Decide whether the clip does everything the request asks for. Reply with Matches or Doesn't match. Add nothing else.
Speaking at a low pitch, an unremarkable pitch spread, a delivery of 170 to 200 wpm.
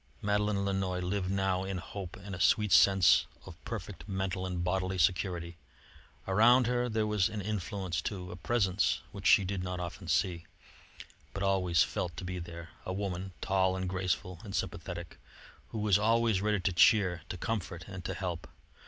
Doesn't match